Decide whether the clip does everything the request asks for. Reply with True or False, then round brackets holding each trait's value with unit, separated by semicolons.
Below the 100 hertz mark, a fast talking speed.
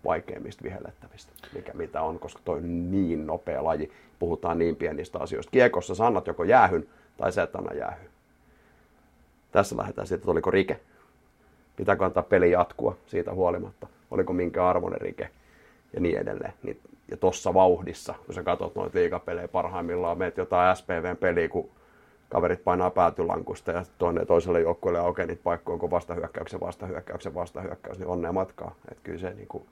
True (90 Hz; 160 wpm)